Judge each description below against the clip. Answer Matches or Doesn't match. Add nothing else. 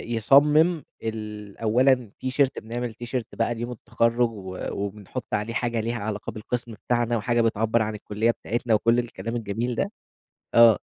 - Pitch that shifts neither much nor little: Doesn't match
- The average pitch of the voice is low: Matches